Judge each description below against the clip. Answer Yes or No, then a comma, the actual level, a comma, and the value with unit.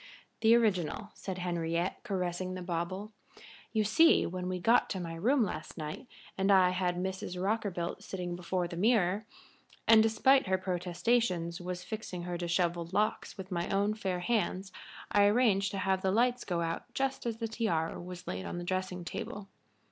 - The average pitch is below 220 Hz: Yes, medium, 185 Hz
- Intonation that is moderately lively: Yes, average, 3.3 semitones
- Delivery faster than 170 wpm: Yes, average, 180 wpm